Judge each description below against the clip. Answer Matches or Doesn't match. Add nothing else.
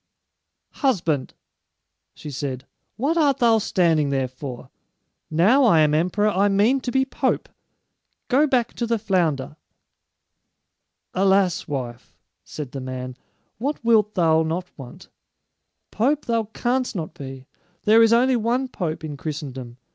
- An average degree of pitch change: Doesn't match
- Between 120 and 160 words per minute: Matches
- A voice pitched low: Doesn't match